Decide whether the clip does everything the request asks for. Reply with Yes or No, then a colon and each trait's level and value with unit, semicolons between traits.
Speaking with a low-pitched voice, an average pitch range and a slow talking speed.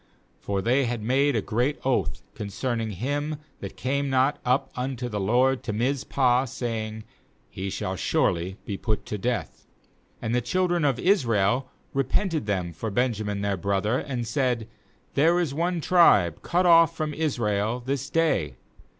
No: low, 125 Hz; average, 4.9 semitones; average, 160 wpm